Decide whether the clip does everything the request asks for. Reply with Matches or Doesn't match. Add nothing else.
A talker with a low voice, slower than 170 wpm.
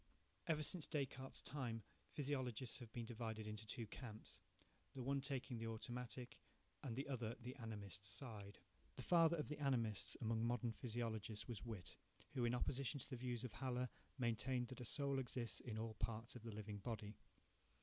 Doesn't match